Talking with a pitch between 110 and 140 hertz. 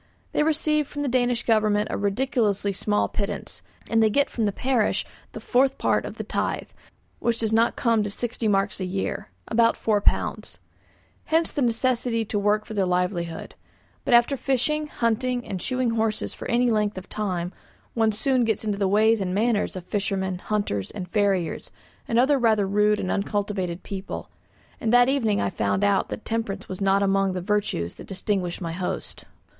No: high, 210 Hz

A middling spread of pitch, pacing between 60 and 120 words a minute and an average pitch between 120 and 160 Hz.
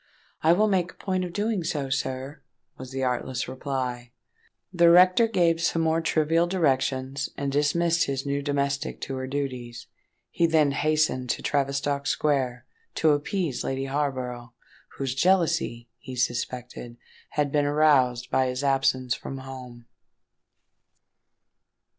No: average, 3.7 semitones; slow, 135 wpm; medium, 140 Hz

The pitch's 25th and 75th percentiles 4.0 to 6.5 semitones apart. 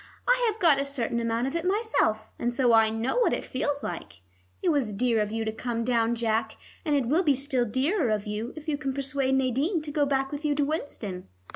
Yes: average, 4.5 semitones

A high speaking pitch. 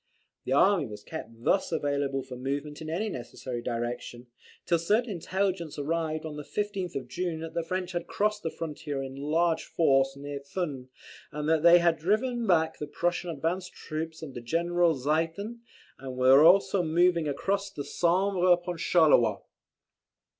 No: medium, 160 Hz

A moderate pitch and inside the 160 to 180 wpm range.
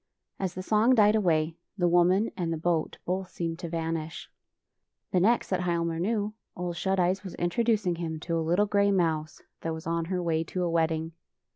No: medium, 175 Hz; average, 195 wpm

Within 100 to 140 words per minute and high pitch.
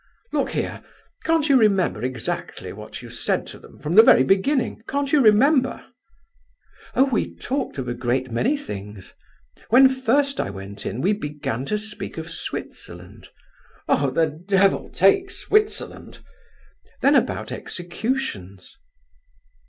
Yes: slow, 135 wpm; high, 195 Hz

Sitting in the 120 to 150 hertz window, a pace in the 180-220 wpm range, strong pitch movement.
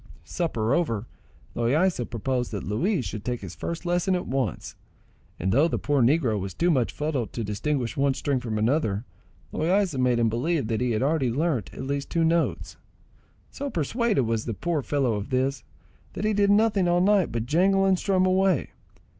Yes: medium, 140 Hz; average, 190 wpm; wide, 7.0 semitones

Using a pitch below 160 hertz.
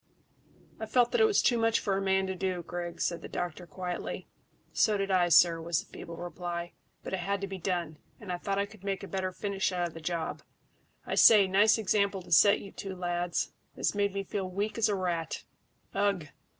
No: high, 190 Hz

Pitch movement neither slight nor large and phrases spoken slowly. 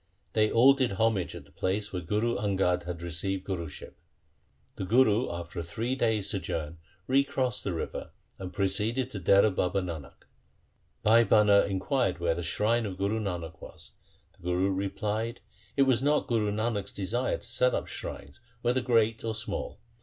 No: average, 4.2 semitones; average, 175 wpm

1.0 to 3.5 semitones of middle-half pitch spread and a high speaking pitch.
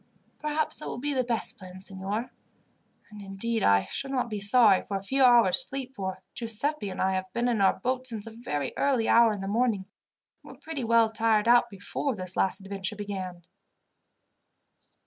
No: average, 4.1 semitones; high, 220 Hz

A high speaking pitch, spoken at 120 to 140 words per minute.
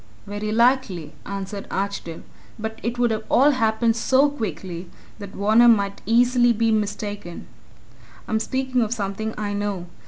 Yes: high, 220 Hz; slow, 135 wpm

